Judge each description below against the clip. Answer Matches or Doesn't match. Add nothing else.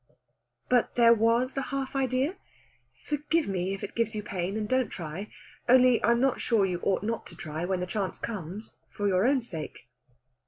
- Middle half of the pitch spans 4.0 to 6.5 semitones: Matches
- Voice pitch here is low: Doesn't match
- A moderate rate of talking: Matches